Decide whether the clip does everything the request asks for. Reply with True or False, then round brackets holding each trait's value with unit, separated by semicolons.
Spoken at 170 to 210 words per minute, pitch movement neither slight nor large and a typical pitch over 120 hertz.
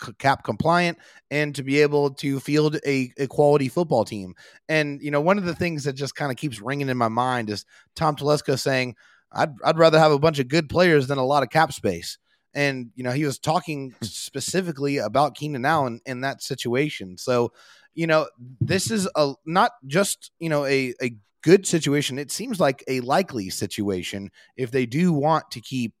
True (200 wpm; 3.5 semitones; 140 Hz)